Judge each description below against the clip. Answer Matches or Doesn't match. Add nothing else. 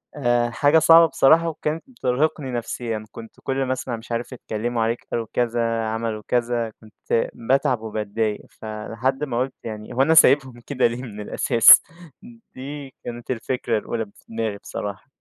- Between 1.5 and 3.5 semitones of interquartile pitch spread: Matches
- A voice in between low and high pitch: Doesn't match